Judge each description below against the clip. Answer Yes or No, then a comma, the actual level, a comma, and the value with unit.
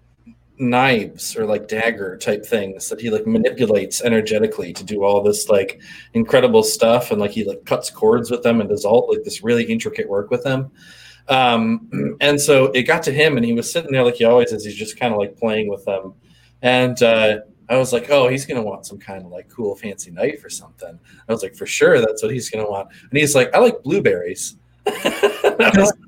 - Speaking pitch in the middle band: No, low, 125 Hz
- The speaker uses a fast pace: Yes, fast, 215 wpm